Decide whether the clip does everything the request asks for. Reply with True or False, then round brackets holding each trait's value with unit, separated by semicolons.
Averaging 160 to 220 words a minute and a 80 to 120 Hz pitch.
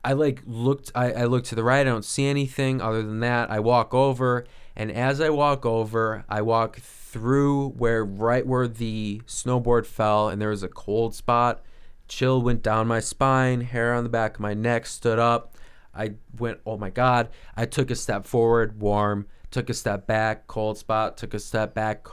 True (200 wpm; 115 Hz)